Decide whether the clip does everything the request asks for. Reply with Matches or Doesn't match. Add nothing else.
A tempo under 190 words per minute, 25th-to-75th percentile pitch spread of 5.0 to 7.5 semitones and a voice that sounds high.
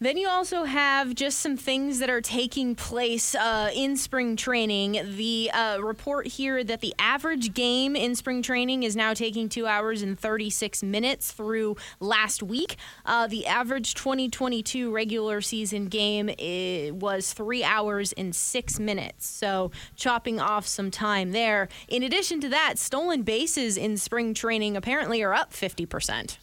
Doesn't match